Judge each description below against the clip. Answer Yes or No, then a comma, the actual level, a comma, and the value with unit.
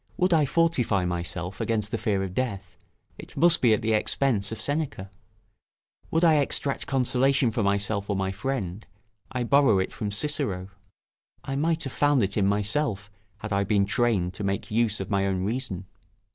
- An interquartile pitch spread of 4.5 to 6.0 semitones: Yes, wide, 5.5 semitones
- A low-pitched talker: Yes, low, 110 Hz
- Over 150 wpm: Yes, average, 180 wpm